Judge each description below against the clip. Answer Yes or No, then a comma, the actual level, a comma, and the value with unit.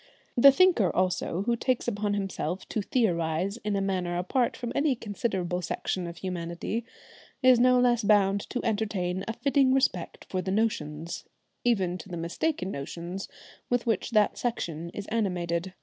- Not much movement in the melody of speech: No, average, 4.9 semitones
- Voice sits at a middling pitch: No, high, 200 Hz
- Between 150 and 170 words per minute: Yes, average, 160 wpm